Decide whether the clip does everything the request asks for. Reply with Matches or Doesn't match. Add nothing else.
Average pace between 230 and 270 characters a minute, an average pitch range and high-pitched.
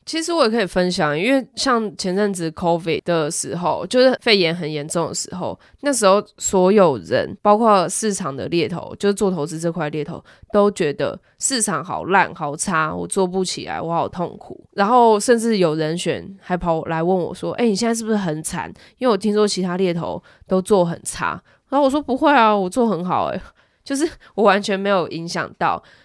Doesn't match